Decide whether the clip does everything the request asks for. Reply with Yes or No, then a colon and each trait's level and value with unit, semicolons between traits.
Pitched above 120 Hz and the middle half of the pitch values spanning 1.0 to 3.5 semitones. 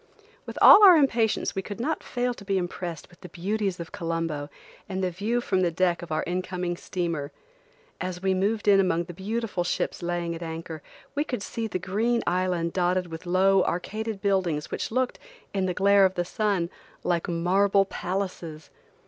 Yes: medium, 185 Hz; average, 2.7 semitones